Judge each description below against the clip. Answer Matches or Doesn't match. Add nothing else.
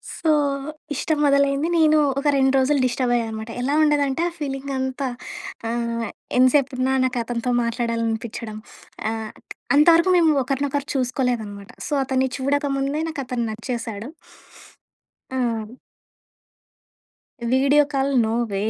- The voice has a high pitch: Matches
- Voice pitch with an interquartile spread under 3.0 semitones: Doesn't match